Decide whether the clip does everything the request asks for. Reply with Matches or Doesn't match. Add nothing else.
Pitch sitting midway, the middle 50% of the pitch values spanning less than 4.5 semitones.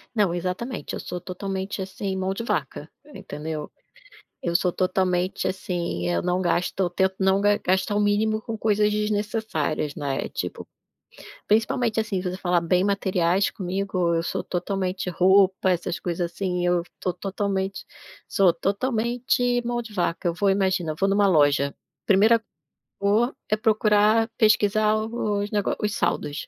Doesn't match